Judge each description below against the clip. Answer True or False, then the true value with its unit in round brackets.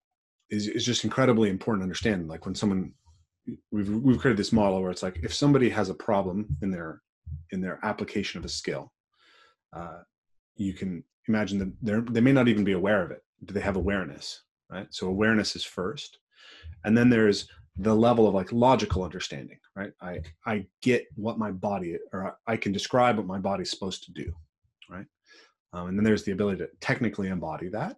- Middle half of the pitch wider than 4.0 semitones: False (3.2 semitones)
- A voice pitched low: True (100 Hz)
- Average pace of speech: True (195 wpm)